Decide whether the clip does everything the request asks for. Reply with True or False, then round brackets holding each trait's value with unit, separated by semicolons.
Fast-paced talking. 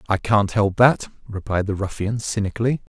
False (165 wpm)